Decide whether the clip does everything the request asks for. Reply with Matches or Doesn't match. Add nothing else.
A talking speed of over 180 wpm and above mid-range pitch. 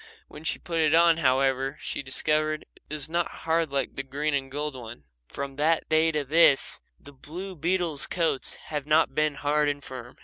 Doesn't match